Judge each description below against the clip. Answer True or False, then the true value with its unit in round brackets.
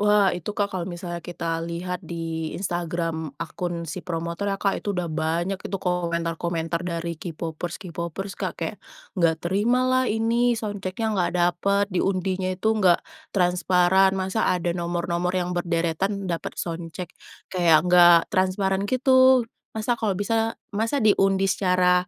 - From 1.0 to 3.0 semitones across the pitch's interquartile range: True (2.7 semitones)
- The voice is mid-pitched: True (180 Hz)